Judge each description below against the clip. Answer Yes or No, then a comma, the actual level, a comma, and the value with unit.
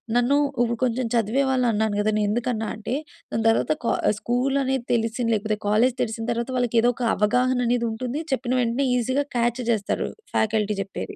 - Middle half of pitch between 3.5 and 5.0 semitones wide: No, narrow, 2.4 semitones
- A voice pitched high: Yes, high, 235 Hz